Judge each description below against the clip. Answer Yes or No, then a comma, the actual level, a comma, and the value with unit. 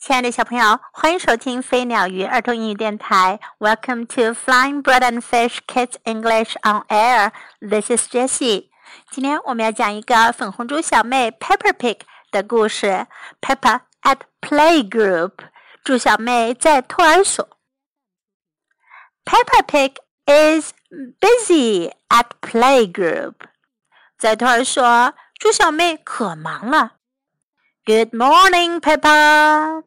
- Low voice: No, very high, 250 Hz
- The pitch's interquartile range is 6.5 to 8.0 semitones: No, average, 5.2 semitones